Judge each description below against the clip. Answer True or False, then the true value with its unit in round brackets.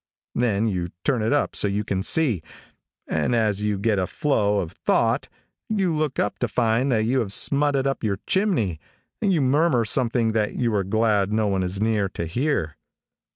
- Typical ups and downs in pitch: True (4.9 semitones)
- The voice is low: True (110 Hz)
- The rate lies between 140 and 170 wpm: False (195 wpm)